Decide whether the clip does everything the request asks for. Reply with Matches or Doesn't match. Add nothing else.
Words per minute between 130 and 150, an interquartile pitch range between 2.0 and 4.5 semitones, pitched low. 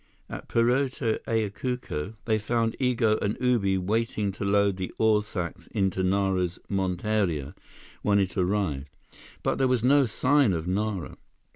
Matches